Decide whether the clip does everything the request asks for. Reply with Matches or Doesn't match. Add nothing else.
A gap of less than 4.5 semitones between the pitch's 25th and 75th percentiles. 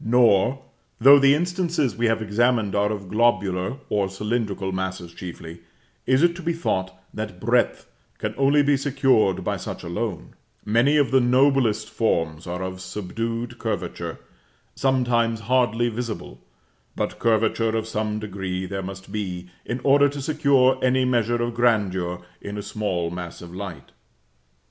Doesn't match